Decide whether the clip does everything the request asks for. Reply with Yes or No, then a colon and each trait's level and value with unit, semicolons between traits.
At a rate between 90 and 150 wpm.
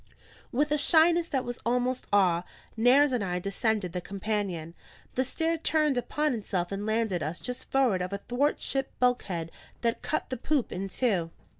No: average, 175 wpm